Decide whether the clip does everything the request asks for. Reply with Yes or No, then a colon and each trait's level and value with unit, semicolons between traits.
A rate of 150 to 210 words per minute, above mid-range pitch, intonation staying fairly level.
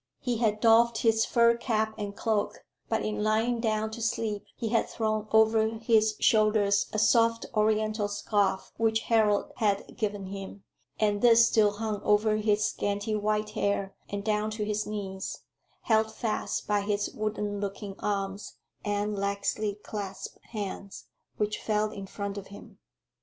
Yes: average, 155 wpm; high, 215 Hz; narrow, 1.3 semitones